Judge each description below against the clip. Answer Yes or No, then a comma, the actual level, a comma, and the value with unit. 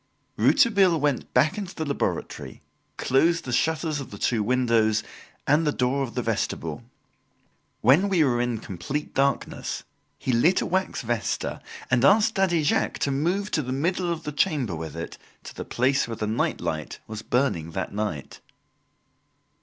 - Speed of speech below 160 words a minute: No, average, 170 wpm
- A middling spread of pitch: No, wide, 6.0 semitones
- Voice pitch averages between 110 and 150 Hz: Yes, low, 135 Hz